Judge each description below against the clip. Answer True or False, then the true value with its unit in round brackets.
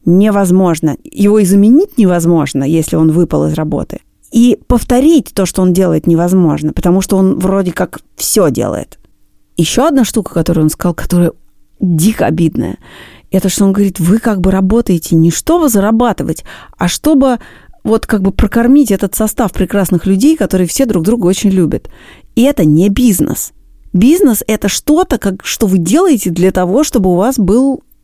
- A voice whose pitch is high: True (195 Hz)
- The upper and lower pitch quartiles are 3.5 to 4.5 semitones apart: False (4.9 semitones)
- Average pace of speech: False (165 wpm)